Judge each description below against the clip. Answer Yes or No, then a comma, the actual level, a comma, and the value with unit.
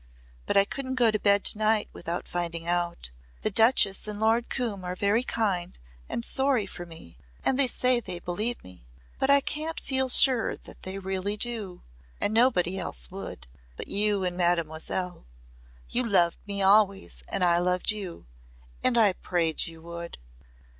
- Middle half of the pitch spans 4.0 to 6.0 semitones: Yes, average, 4.6 semitones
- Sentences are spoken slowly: No, average, 165 wpm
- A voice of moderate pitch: No, high, 195 Hz